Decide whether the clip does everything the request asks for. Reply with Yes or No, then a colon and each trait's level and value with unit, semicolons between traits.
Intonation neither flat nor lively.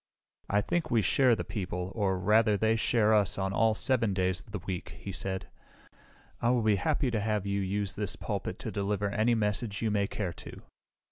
No: narrow, 2.2 semitones